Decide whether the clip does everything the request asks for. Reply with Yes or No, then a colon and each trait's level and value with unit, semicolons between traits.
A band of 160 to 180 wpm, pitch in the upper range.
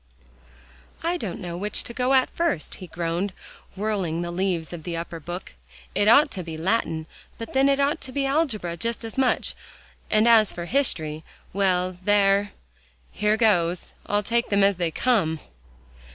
Yes: average, 170 wpm; high, 200 Hz